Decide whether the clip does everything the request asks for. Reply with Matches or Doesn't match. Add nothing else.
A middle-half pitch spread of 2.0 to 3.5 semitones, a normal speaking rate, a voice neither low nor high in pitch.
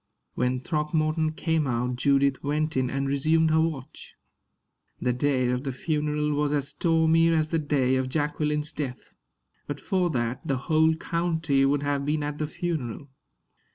Matches